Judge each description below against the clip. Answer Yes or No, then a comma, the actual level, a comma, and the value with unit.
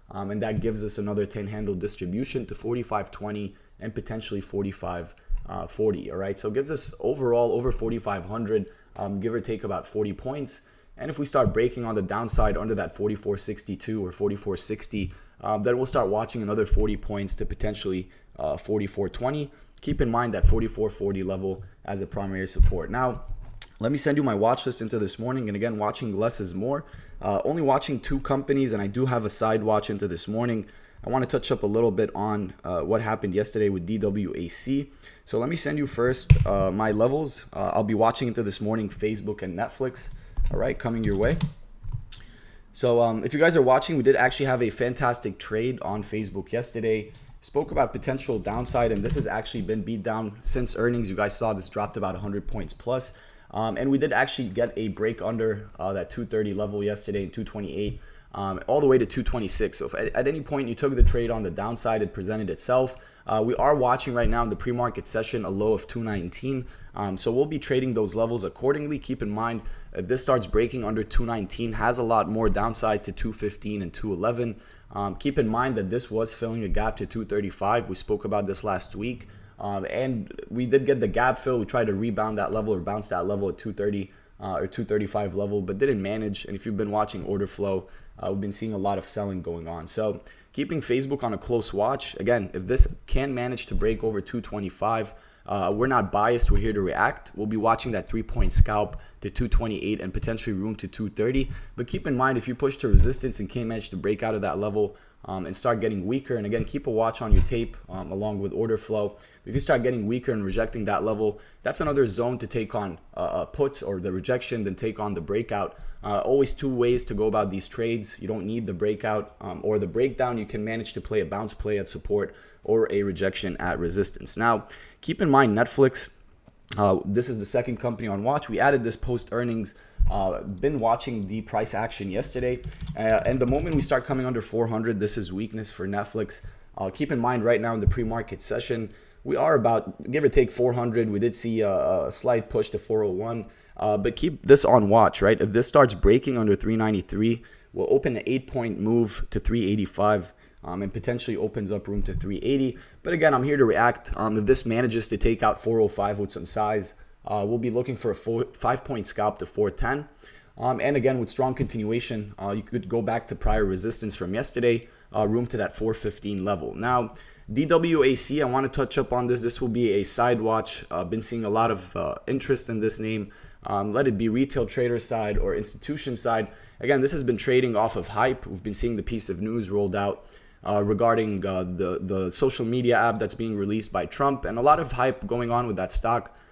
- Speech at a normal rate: No, fast, 215 wpm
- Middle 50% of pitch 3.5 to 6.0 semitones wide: No, average, 3.0 semitones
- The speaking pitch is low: Yes, low, 110 Hz